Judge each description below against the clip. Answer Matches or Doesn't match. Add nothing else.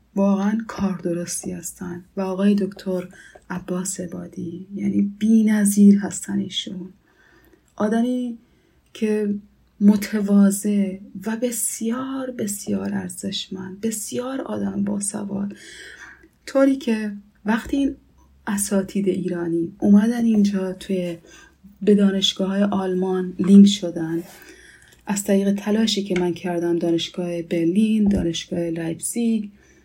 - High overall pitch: Matches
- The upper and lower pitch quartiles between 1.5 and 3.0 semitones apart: Matches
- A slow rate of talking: Matches